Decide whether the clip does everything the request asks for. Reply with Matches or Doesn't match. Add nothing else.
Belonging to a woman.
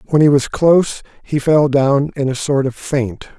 Doesn't match